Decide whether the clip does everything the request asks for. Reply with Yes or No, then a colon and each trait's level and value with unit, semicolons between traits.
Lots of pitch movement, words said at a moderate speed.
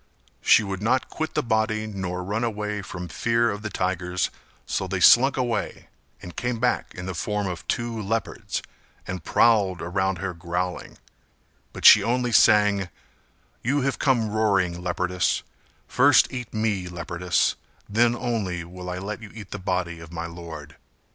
No: average, 4.0 semitones; average, 160 wpm